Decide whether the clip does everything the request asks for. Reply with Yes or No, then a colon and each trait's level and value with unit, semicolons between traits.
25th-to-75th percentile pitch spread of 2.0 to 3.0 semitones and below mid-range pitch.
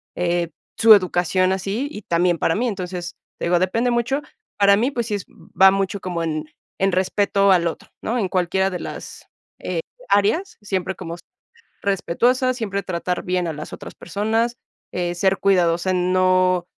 No: average, 2.7 semitones; high, 190 Hz